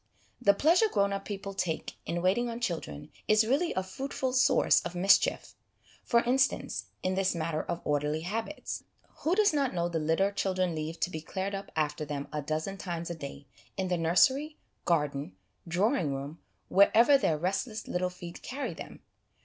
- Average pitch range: No, wide, 5.8 semitones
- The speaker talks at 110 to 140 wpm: No, average, 180 wpm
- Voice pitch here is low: No, medium, 185 Hz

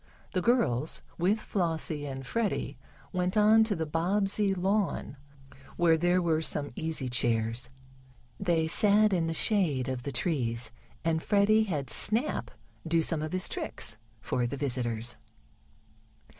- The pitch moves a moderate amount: No, wide, 6.7 semitones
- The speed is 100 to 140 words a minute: Yes, slow, 135 wpm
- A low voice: No, medium, 165 Hz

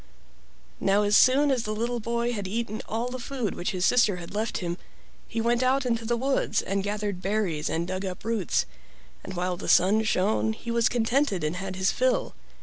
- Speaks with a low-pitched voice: No, high, 215 Hz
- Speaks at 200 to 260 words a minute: Yes, fast, 205 wpm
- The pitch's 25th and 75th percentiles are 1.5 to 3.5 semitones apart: No, average, 4.0 semitones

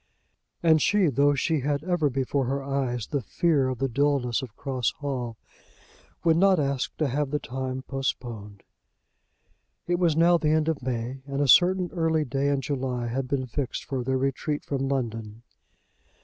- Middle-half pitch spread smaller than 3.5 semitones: Yes, average, 2.9 semitones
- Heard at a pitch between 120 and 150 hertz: Yes, low, 135 Hz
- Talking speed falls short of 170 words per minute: No, average, 175 wpm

